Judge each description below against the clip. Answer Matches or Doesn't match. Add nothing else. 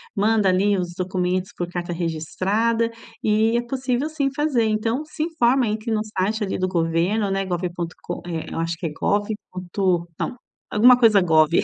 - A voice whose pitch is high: Matches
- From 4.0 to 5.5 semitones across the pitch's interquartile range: Matches